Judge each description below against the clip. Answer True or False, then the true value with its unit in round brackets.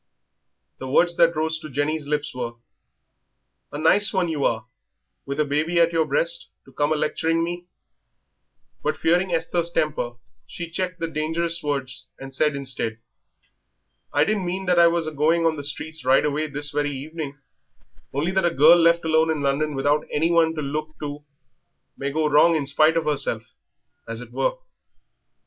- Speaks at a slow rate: False (175 wpm)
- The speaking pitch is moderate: True (155 Hz)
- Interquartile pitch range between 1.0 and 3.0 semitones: True (2.7 semitones)